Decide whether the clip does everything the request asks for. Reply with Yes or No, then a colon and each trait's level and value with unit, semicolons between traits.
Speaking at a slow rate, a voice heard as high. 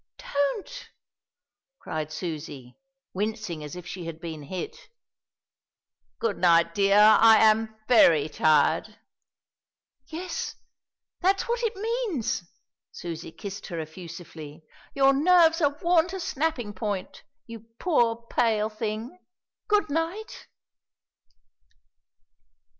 Yes: slow, 105 wpm; high, 220 Hz